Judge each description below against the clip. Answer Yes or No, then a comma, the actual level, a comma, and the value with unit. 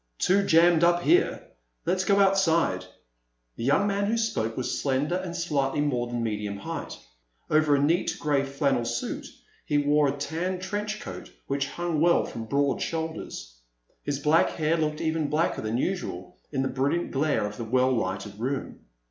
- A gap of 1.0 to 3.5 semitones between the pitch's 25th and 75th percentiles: No, average, 5.0 semitones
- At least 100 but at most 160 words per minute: No, average, 175 wpm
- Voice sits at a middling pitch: Yes, medium, 145 Hz